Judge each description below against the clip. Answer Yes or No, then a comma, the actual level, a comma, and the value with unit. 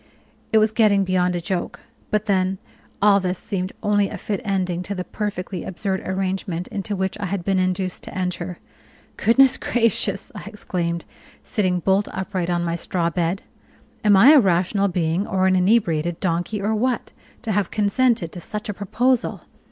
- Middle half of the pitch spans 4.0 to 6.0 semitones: No, narrow, 2.5 semitones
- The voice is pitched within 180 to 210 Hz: Yes, high, 190 Hz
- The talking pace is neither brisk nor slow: Yes, average, 175 wpm